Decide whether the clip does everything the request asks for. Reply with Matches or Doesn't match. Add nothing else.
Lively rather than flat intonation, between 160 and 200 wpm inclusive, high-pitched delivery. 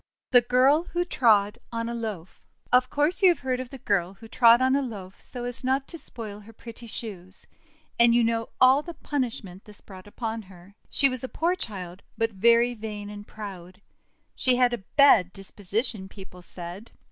Doesn't match